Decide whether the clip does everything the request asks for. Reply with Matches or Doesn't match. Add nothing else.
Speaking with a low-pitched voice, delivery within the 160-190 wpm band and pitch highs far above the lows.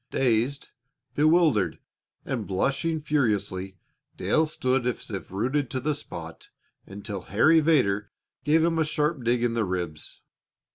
Doesn't match